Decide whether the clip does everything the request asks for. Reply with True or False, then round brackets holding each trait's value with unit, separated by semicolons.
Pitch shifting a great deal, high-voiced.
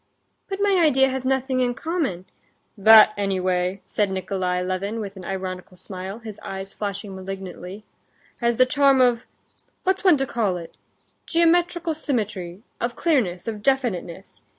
True (6.0 semitones; 215 Hz)